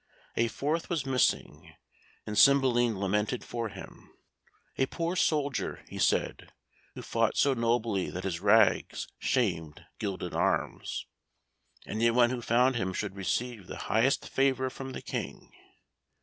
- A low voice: Yes, low, 120 Hz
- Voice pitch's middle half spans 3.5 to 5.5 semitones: Yes, average, 4.3 semitones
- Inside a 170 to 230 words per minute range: No, slow, 135 wpm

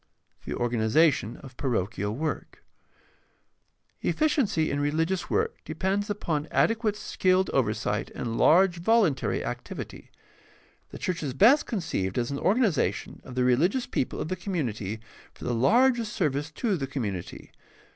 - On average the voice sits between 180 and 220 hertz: No, medium, 155 Hz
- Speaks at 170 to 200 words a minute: No, average, 140 wpm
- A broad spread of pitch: Yes, wide, 8.2 semitones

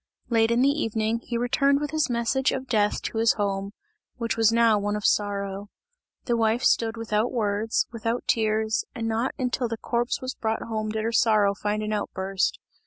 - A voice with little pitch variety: Yes, narrow, 2.0 semitones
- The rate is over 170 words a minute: Yes, average, 190 wpm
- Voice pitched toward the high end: Yes, high, 225 Hz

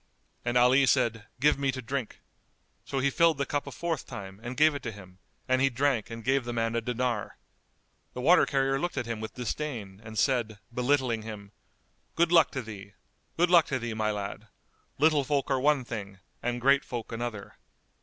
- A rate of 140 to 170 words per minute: No, average, 200 wpm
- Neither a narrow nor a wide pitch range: Yes, average, 3.9 semitones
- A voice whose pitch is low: Yes, low, 125 Hz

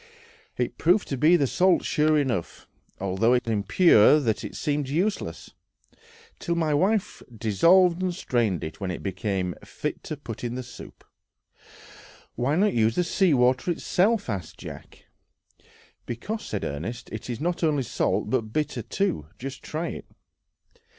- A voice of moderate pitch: No, low, 130 Hz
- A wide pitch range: Yes, wide, 7.6 semitones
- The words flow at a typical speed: Yes, average, 150 wpm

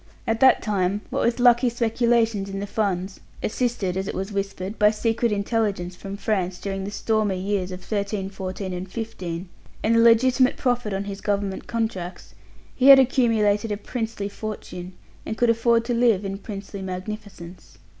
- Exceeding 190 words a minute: No, average, 165 wpm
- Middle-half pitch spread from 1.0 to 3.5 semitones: Yes, average, 3.0 semitones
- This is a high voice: Yes, high, 205 Hz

